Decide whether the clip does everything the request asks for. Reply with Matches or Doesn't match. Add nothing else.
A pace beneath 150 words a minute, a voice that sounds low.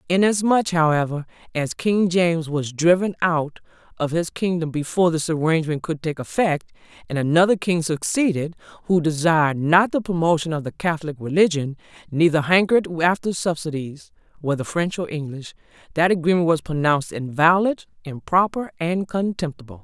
Doesn't match